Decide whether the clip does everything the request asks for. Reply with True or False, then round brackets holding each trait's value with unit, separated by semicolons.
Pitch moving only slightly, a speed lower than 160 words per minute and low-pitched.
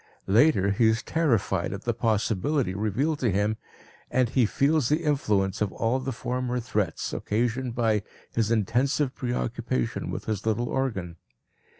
False (4.0 semitones; 150 wpm; 115 Hz)